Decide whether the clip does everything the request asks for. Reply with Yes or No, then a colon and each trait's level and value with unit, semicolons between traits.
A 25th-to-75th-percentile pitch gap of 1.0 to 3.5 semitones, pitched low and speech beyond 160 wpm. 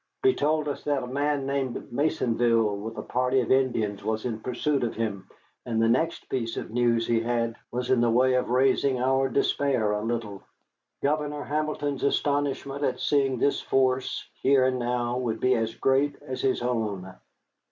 Yes: average, 3.2 semitones; low, 125 Hz; average, 180 wpm